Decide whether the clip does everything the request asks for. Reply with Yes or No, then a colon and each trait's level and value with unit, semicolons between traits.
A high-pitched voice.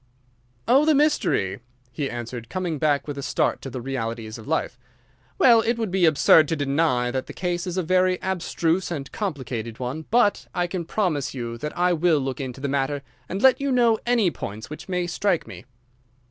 No: medium, 160 Hz